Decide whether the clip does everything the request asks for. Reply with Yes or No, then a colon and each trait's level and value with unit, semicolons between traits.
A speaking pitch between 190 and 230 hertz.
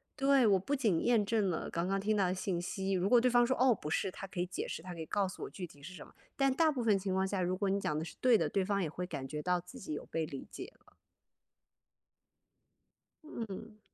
Yes: high, 195 Hz